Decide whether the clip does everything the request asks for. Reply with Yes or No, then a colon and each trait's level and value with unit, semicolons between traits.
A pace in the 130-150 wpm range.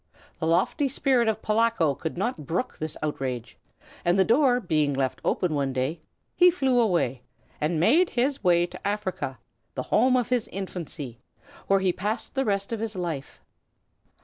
No: average, 170 wpm